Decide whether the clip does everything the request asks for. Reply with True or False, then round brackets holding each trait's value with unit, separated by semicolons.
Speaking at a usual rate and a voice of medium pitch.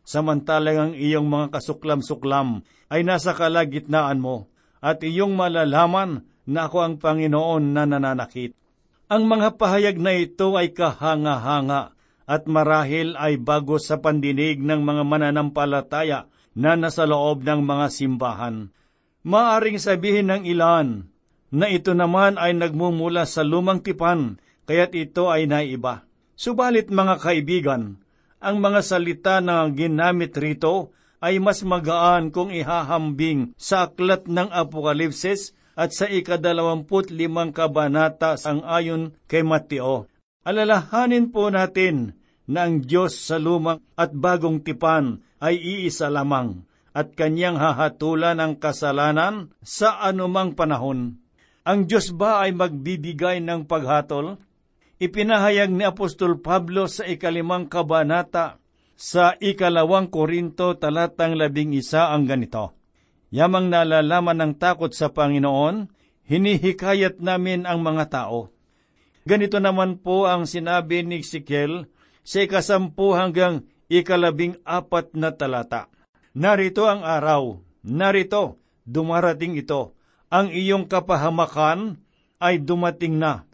True (120 wpm; 165 Hz)